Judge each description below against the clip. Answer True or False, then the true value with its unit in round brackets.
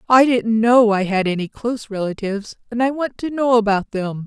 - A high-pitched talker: True (225 Hz)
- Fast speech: True (210 wpm)